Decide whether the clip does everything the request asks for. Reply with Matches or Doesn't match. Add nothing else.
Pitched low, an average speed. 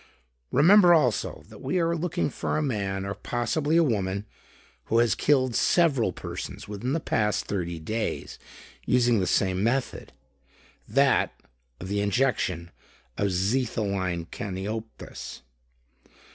Doesn't match